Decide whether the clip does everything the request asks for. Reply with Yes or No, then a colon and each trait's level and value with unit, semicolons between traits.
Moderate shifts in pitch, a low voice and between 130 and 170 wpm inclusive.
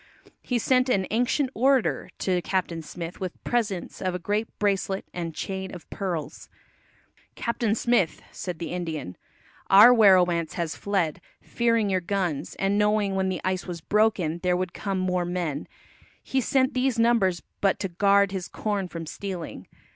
No: average, 3.4 semitones; high, 190 Hz; average, 160 wpm